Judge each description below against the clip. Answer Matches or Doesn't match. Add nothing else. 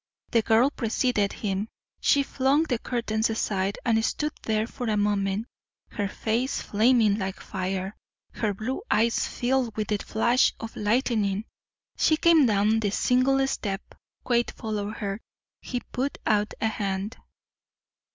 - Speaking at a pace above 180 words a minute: Doesn't match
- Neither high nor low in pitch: Doesn't match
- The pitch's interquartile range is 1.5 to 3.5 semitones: Matches